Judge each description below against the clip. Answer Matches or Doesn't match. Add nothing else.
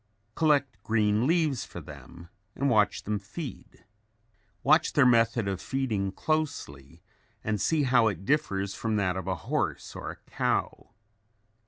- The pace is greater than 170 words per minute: Doesn't match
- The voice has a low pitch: Matches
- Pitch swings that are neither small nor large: Doesn't match